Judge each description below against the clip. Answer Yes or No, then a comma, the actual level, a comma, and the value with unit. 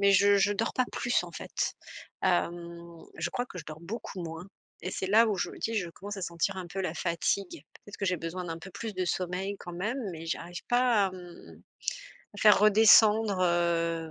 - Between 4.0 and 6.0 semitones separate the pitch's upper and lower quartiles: No, average, 3.2 semitones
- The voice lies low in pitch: No, medium, 185 Hz